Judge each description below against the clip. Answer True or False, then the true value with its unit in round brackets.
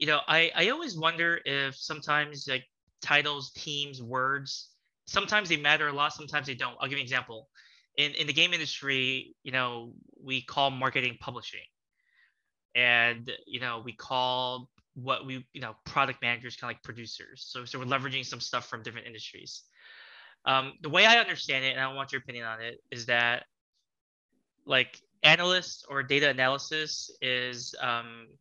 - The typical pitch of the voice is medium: False (130 Hz)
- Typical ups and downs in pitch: True (3.2 semitones)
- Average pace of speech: True (175 wpm)